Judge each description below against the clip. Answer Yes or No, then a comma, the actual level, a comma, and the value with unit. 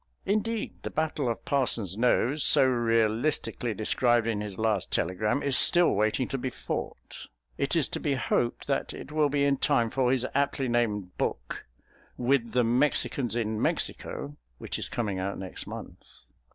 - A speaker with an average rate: Yes, average, 165 wpm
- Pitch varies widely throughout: No, average, 4.3 semitones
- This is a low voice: Yes, low, 120 Hz